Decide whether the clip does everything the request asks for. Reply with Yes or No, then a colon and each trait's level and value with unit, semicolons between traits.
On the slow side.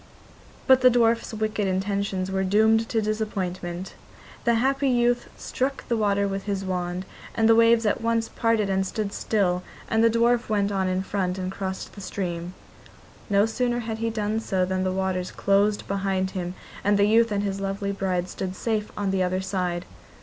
No: average, 185 wpm